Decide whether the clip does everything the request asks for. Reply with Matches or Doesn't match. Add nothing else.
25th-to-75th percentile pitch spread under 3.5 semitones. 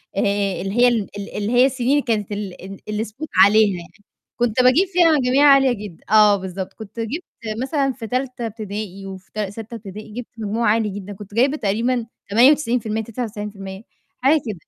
Doesn't match